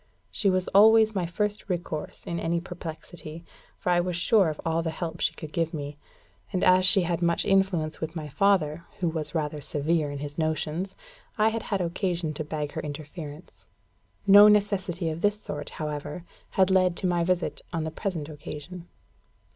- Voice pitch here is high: No, medium, 170 Hz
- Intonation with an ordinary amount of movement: Yes, average, 3.3 semitones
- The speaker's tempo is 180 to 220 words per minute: Yes, average, 185 wpm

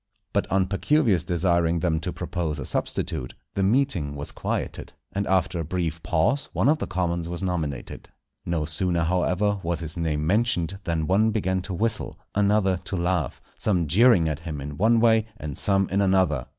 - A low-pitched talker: Yes, very low, 90 Hz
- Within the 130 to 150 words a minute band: No, average, 180 wpm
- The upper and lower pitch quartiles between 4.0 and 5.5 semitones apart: No, average, 3.5 semitones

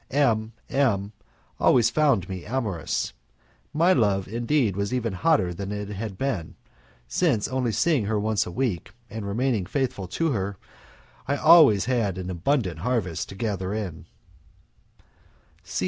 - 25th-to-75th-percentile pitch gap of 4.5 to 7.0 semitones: Yes, average, 5.2 semitones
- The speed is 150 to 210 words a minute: No, average, 140 wpm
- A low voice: Yes, low, 110 Hz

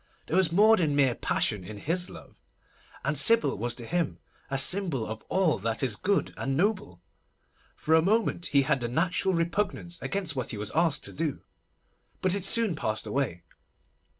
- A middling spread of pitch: No, wide, 7.3 semitones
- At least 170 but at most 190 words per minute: Yes, average, 180 wpm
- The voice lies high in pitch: No, medium, 160 Hz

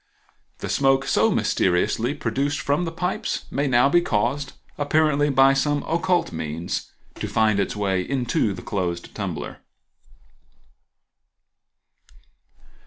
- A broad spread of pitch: Yes, wide, 5.9 semitones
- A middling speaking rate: No, slow, 115 wpm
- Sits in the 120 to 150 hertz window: Yes, low, 135 Hz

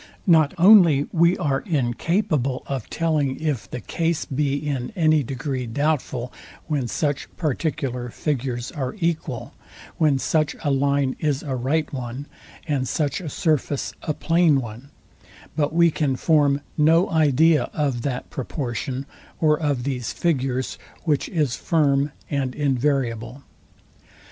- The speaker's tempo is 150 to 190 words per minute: No, slow, 135 wpm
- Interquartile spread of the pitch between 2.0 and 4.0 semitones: Yes, average, 3.2 semitones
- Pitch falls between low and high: Yes, medium, 145 Hz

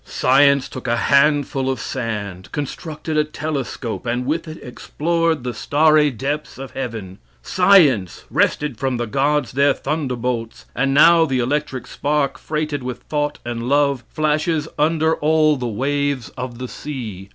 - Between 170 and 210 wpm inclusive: No, average, 150 wpm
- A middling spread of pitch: Yes, average, 3.4 semitones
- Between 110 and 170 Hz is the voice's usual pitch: Yes, medium, 140 Hz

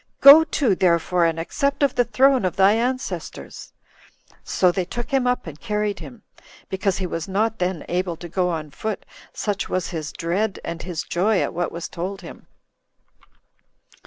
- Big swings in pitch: No, average, 4.7 semitones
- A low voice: No, high, 190 Hz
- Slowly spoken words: No, average, 175 wpm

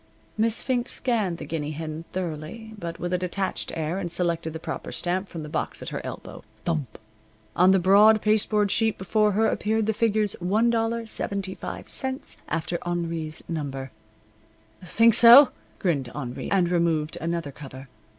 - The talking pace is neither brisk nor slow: Yes, average, 150 wpm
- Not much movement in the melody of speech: No, average, 5.0 semitones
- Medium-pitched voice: Yes, medium, 180 Hz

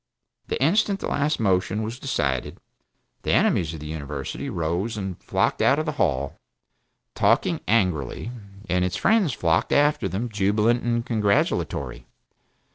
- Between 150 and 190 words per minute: No, average, 140 wpm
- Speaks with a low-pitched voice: Yes, low, 100 Hz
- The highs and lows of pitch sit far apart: Yes, wide, 6.9 semitones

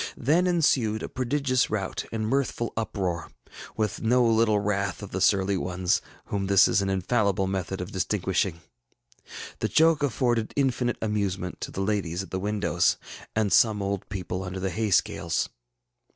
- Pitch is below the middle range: Yes, low, 100 Hz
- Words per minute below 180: Yes, average, 160 wpm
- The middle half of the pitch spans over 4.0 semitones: No, average, 3.5 semitones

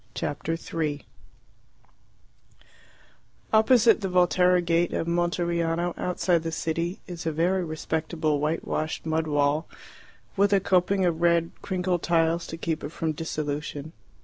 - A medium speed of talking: No, slow, 130 wpm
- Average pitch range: No, narrow, 2.1 semitones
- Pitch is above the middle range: No, medium, 165 Hz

